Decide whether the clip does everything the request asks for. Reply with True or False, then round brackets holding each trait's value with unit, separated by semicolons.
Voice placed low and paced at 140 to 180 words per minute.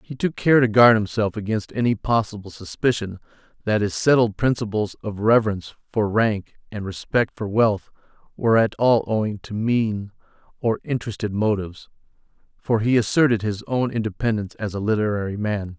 True (110 Hz; 155 wpm)